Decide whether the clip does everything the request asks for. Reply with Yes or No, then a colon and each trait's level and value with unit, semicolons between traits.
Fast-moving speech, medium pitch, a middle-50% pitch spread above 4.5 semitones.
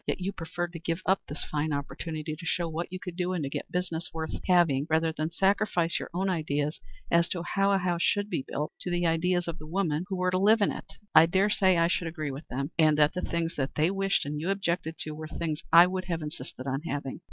No: fast, 255 wpm; medium, 170 Hz; average, 2.8 semitones